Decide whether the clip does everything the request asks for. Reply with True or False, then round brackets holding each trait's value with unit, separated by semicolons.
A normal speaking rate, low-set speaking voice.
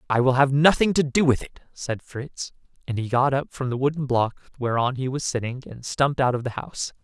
False (240 wpm; 130 Hz)